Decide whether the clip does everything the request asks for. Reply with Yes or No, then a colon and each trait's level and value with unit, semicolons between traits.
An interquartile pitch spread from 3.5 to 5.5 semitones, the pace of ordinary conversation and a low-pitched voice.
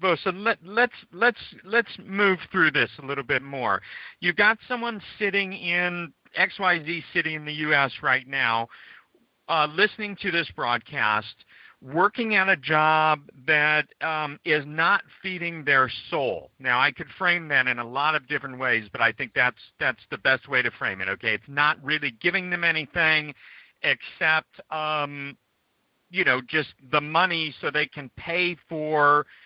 No: average, 4.3 semitones; average, 170 wpm; medium, 155 Hz